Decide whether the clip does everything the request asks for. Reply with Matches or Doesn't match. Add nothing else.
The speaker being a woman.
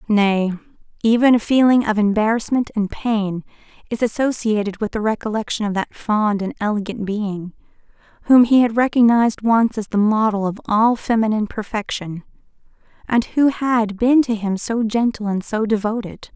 Matches